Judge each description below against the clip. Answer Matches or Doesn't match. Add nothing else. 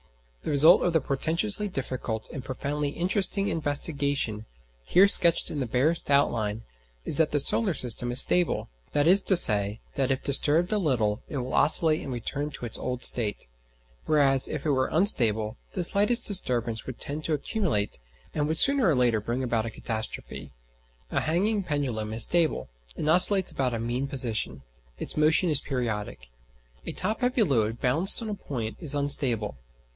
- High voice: Doesn't match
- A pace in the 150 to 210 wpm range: Matches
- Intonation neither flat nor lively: Doesn't match